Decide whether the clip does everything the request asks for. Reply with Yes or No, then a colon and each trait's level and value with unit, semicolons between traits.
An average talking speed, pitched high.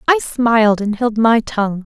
Yes: average, 180 wpm; high, 225 Hz